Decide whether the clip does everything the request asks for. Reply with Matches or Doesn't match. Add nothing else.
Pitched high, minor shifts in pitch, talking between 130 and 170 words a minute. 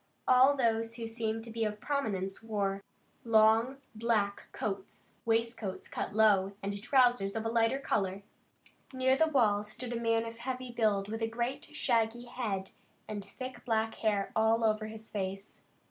Matches